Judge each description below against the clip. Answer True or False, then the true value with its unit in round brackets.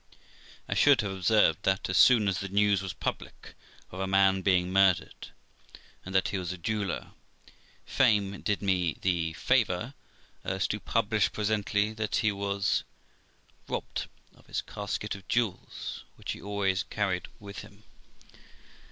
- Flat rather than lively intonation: True (1.9 semitones)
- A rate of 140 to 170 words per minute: True (150 wpm)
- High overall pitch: False (100 Hz)